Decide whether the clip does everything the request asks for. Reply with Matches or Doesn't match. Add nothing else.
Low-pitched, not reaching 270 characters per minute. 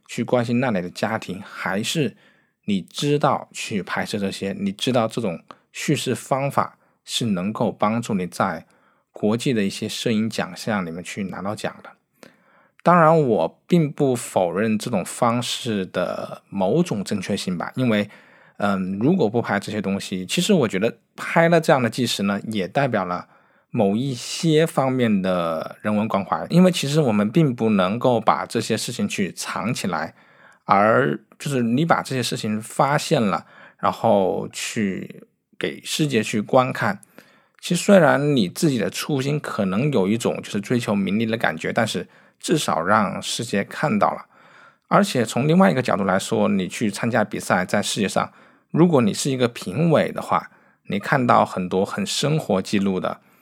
Matches